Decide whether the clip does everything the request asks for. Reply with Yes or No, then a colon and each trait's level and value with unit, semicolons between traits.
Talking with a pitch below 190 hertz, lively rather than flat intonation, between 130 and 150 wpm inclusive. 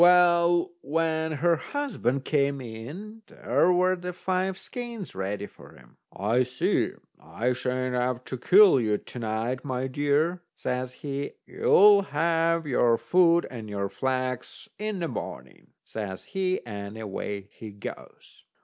Yes: medium, 140 Hz; wide, 6.9 semitones; average, 140 wpm